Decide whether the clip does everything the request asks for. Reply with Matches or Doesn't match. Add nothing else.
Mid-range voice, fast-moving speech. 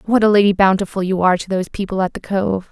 Doesn't match